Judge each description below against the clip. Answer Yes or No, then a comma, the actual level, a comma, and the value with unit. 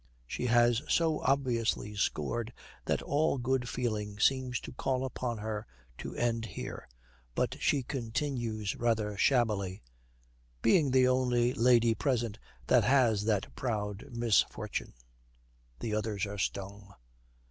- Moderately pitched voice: No, low, 115 Hz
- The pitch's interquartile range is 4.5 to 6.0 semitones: No, average, 3.3 semitones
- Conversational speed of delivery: No, slow, 125 wpm